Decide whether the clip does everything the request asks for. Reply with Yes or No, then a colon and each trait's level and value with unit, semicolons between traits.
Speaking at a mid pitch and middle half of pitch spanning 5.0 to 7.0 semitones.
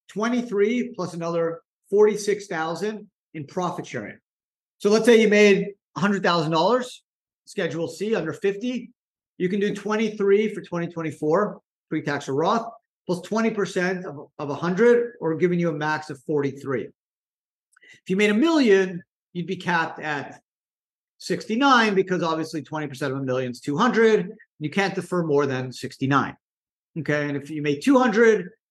Yes: medium, 180 Hz; wide, 5.4 semitones